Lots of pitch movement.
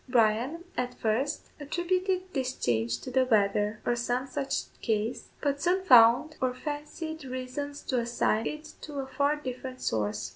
No: average, 4.2 semitones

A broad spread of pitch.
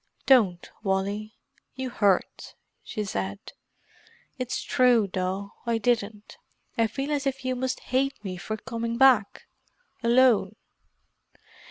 No: average, 4.3 semitones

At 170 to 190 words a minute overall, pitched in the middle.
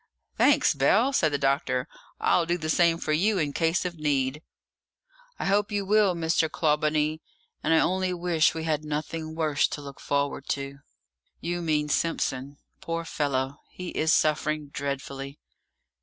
No: average, 155 wpm; medium, 155 Hz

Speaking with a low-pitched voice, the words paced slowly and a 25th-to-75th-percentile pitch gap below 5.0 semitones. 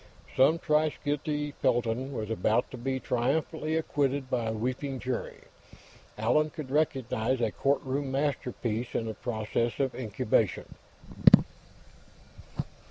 Yes: low, 130 Hz; slow, 115 wpm; average, 3.7 semitones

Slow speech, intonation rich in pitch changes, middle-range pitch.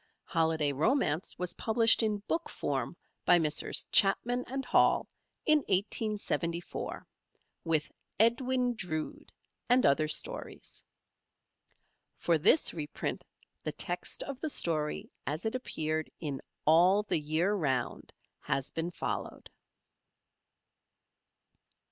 Yes: slow, 105 wpm; wide, 6.6 semitones; medium, 175 Hz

